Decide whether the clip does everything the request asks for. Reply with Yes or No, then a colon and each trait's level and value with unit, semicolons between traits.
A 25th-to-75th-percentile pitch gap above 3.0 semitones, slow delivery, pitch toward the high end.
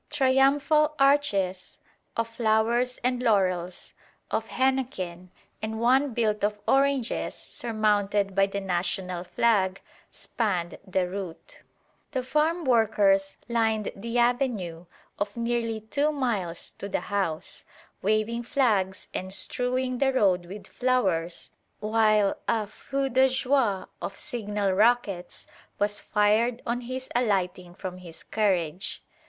Yes: average, 4.5 semitones; slow, 120 wpm; high, 215 Hz